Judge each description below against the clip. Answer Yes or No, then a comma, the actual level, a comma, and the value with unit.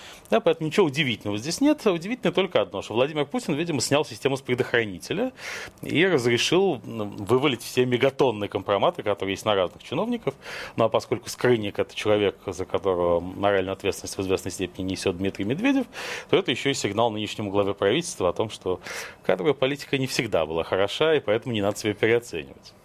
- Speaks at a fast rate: Yes, fast, 175 wpm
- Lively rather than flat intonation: Yes, wide, 7.0 semitones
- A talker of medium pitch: No, low, 120 Hz